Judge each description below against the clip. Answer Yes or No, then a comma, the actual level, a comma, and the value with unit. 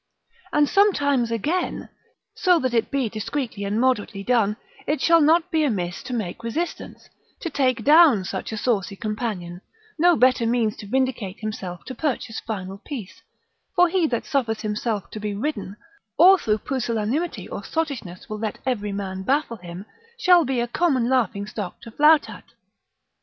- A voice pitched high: Yes, high, 235 Hz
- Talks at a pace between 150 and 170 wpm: Yes, average, 165 wpm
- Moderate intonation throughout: No, wide, 5.8 semitones